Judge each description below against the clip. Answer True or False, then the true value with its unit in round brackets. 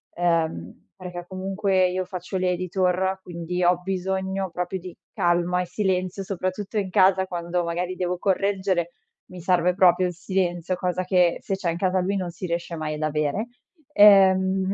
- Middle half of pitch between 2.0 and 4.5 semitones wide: False (1.4 semitones)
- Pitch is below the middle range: False (185 Hz)